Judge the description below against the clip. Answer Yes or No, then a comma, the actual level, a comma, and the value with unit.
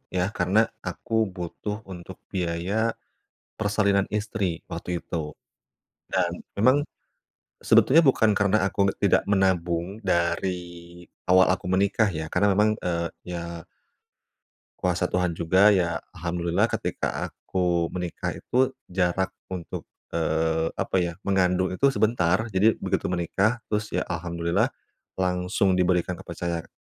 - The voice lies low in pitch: Yes, very low, 90 Hz